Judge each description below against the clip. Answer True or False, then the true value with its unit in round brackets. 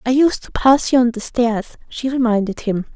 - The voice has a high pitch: True (240 Hz)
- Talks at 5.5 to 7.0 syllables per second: False (5.1 syllables/s)